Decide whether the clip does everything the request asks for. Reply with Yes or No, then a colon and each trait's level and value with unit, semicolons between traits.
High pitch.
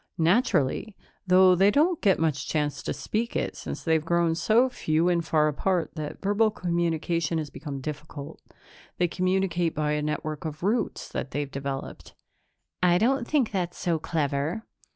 No: medium, 170 Hz